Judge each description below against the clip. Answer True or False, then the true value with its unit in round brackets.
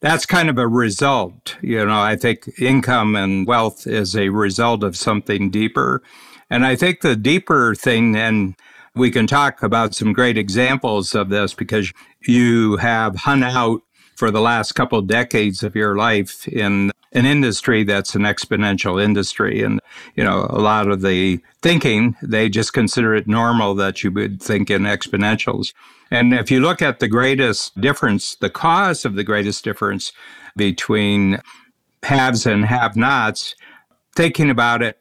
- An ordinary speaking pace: True (165 wpm)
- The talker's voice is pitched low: True (110 Hz)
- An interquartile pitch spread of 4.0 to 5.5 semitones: False (3.3 semitones)